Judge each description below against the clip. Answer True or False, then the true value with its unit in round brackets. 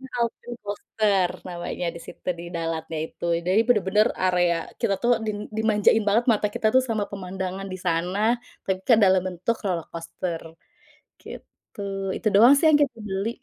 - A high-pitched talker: True (195 Hz)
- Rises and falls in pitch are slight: False (3.6 semitones)